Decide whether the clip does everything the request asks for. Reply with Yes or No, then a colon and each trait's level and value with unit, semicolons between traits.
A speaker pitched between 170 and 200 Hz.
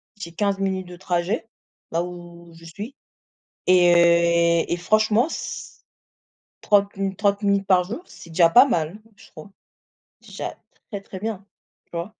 Yes: medium, 185 Hz